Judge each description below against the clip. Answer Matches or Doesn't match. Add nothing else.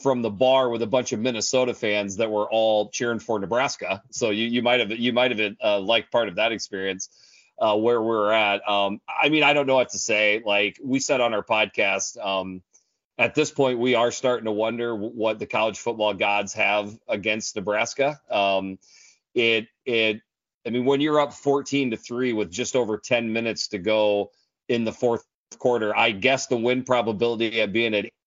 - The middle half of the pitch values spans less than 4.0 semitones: Matches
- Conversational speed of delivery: Doesn't match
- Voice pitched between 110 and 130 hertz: Matches